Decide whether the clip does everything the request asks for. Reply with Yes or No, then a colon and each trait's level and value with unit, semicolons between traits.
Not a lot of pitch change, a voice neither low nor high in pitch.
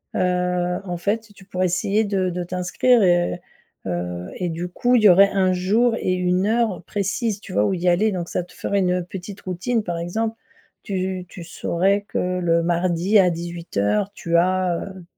Yes: narrow, 2.3 semitones; medium, 180 Hz